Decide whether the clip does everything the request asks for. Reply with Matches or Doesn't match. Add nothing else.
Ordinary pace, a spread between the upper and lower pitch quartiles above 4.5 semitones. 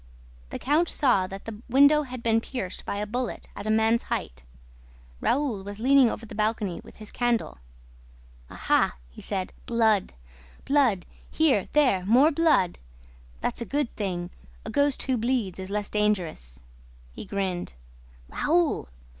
Matches